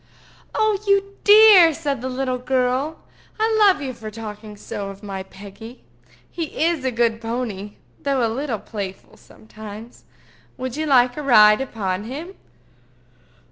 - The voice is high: Yes, very high, 250 Hz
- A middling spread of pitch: No, wide, 5.8 semitones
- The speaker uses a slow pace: No, average, 145 wpm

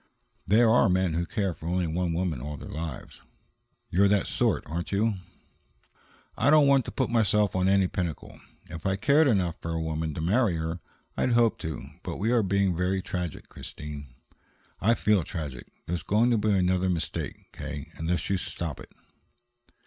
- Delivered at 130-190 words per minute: Yes, average, 180 wpm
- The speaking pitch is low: Yes, very low, 90 Hz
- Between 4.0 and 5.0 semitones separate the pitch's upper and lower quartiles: Yes, average, 4.4 semitones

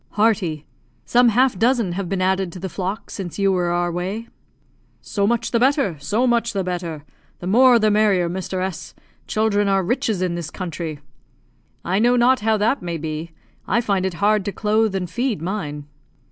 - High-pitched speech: Yes, high, 195 Hz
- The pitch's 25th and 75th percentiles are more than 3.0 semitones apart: Yes, average, 3.9 semitones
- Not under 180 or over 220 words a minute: Yes, average, 190 wpm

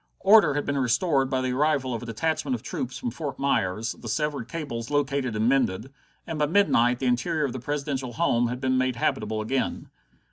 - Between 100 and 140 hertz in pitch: Yes, low, 135 Hz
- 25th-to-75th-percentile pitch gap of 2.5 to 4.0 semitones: Yes, average, 3.6 semitones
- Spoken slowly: No, fast, 205 wpm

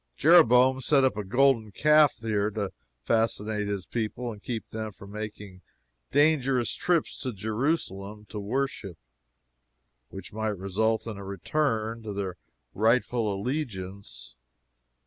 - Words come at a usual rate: No, slow, 125 wpm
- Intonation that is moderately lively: Yes, average, 4.1 semitones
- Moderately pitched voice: No, low, 110 Hz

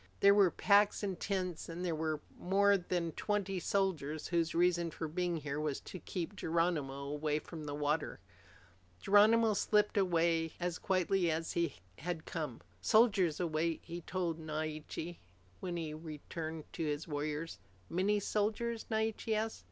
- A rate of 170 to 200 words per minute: No, average, 155 wpm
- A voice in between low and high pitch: Yes, medium, 170 Hz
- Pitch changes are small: No, average, 3.7 semitones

